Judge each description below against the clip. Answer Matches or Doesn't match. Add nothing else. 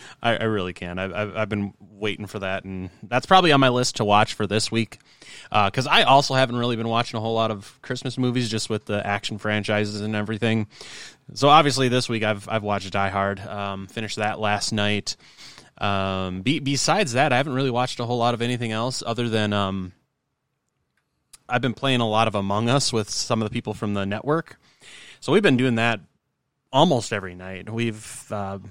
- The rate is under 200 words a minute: Doesn't match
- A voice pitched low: Matches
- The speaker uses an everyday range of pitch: Matches